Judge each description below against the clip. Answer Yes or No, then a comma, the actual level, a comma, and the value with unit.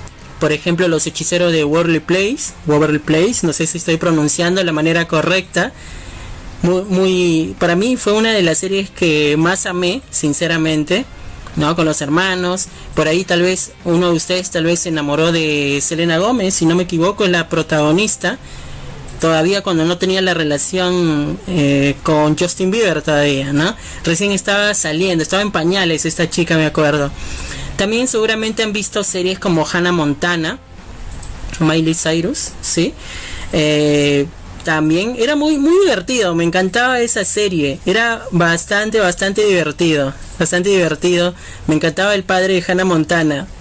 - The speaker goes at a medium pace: Yes, average, 155 wpm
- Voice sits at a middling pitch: Yes, medium, 170 Hz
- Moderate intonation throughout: Yes, average, 3.2 semitones